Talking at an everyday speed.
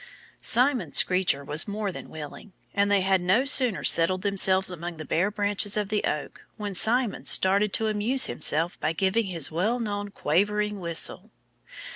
Yes: average, 165 wpm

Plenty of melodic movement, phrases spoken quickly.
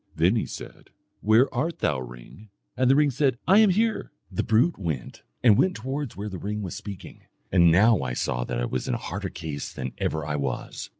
Yes: wide, 8.7 semitones; fast, 220 wpm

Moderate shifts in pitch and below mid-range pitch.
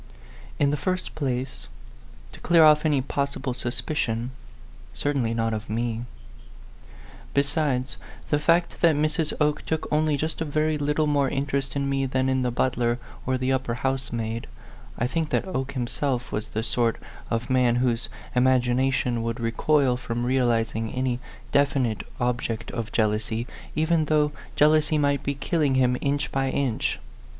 Yes: average, 3.4 semitones; low, 130 Hz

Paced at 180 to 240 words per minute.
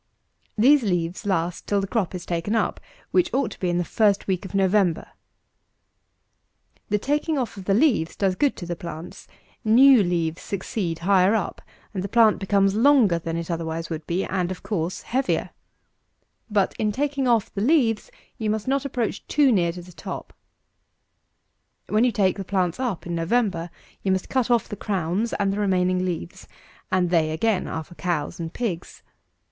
Yes: average, 185 wpm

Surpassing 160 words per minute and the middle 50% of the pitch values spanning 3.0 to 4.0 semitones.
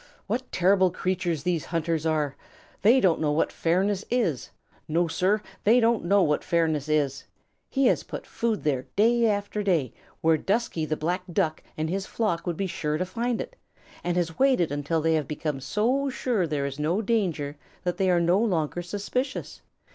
No: average, 185 wpm; average, 5.0 semitones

